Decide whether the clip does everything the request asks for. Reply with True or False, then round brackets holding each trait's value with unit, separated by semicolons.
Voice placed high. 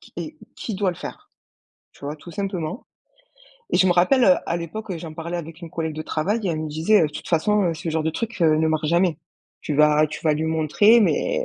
False (170 Hz)